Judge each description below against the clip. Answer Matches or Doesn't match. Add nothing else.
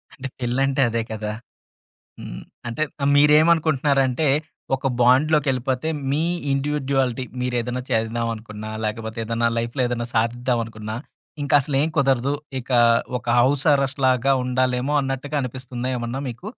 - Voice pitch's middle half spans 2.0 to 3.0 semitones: Matches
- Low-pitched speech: Matches